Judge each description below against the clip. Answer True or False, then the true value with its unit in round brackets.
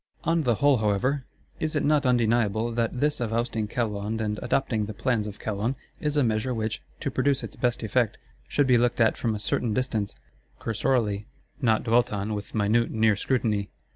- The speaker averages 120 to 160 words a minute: False (190 wpm)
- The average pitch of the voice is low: True (115 Hz)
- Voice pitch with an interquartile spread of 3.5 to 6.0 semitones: False (3.0 semitones)